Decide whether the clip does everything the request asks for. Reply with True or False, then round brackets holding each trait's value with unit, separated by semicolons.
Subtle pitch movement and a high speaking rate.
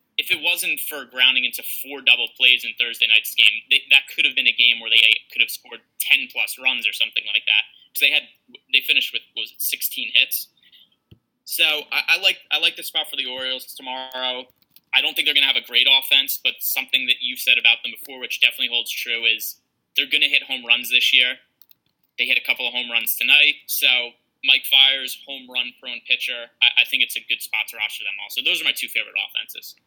True (1.8 semitones; 240 wpm)